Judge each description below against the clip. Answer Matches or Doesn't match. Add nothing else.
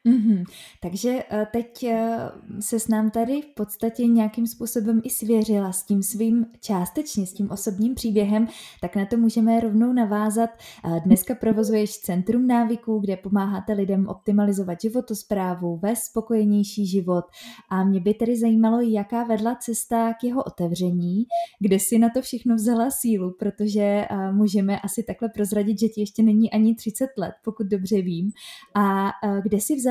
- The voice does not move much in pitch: Matches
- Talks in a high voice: Matches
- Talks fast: Doesn't match